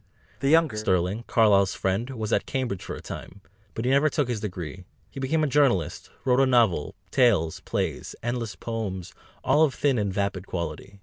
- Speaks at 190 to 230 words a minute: No, average, 180 wpm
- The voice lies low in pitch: Yes, low, 110 Hz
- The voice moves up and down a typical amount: No, wide, 5.7 semitones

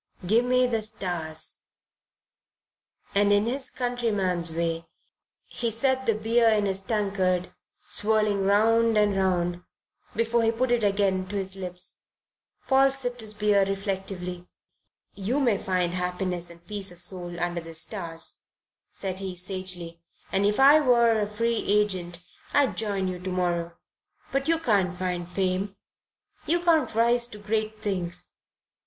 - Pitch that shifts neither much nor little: Yes, average, 3.9 semitones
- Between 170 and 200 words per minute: No, average, 140 wpm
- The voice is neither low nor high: No, high, 200 Hz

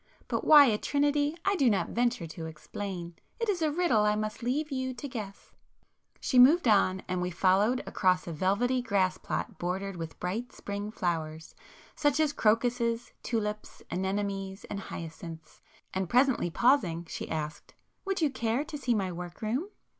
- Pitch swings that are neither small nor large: No, wide, 6.0 semitones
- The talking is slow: No, average, 160 wpm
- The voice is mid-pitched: No, high, 210 Hz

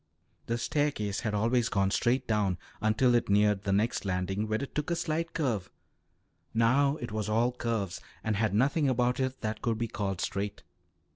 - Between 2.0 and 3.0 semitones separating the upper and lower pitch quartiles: No, average, 3.6 semitones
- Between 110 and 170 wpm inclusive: No, average, 185 wpm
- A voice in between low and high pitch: No, low, 110 Hz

